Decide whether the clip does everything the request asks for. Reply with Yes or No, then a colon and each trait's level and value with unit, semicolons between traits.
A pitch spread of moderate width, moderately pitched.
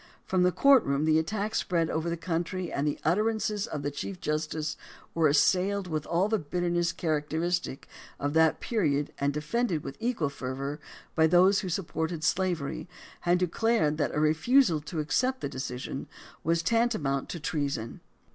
Yes: average, 3.8 semitones; medium, 165 Hz